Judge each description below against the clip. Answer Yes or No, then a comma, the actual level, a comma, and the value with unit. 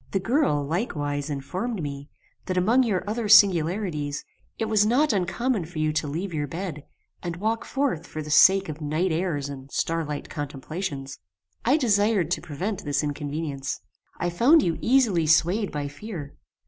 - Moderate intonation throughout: No, wide, 6.1 semitones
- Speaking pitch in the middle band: Yes, medium, 170 Hz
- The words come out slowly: No, average, 160 wpm